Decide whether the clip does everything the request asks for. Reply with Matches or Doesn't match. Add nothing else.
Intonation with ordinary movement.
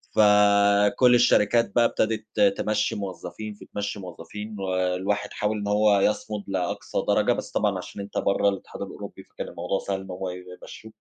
Doesn't match